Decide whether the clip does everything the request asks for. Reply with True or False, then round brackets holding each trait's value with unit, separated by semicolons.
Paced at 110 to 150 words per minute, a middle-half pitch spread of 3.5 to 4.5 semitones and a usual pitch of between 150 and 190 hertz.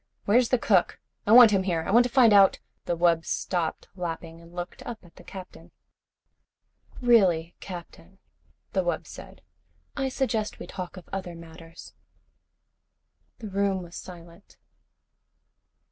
True (145 wpm; 4.0 semitones; 185 Hz)